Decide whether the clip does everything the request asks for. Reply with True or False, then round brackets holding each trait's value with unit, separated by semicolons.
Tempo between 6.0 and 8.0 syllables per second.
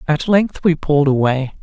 False (5.0 syllables/s)